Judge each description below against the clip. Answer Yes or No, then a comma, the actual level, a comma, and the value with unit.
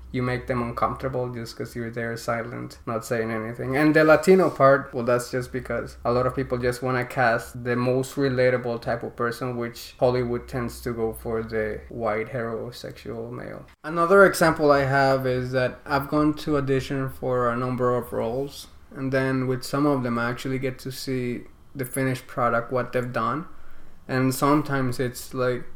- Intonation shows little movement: Yes, narrow, 2.0 semitones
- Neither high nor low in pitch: No, low, 125 Hz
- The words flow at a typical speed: Yes, average, 185 wpm